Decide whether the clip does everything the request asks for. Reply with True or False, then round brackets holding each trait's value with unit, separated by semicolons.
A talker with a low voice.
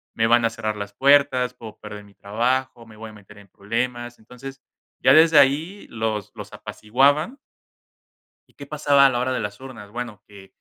True (120 Hz)